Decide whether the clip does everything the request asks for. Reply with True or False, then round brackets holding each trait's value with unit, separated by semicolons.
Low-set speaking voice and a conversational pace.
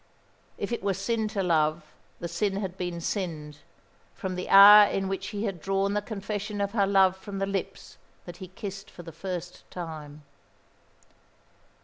False (195 Hz; 170 wpm)